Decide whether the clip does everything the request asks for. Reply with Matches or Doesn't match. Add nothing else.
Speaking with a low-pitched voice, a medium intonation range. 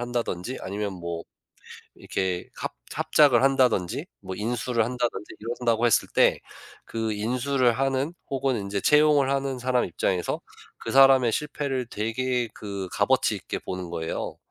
Matches